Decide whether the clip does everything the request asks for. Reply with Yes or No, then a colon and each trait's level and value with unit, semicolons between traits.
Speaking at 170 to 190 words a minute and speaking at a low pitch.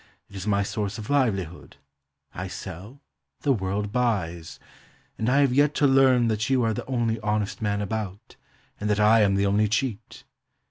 Yes: average, 180 wpm; low, 105 Hz